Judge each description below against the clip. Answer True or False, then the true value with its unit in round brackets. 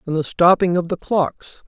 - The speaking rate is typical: False (215 wpm)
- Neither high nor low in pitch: True (175 Hz)